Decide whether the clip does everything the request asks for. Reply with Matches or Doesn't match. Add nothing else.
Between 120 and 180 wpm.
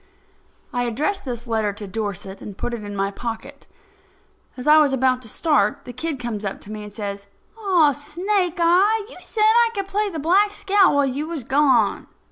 Doesn't match